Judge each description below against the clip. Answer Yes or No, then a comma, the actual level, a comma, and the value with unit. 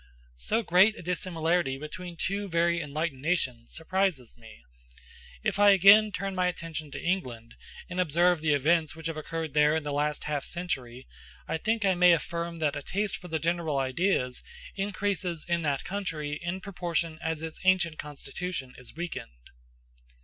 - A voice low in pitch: No, medium, 165 Hz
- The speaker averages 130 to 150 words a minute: No, average, 165 wpm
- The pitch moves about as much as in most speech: Yes, average, 3.5 semitones